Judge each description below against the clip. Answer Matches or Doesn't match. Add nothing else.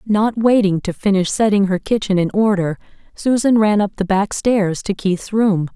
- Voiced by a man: Doesn't match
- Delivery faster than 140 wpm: Matches